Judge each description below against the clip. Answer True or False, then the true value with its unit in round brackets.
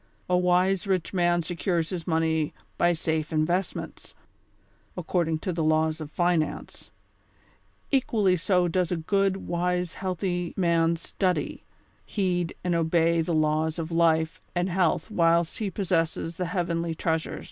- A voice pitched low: False (170 Hz)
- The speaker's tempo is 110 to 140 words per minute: True (135 wpm)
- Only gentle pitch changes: True (1.9 semitones)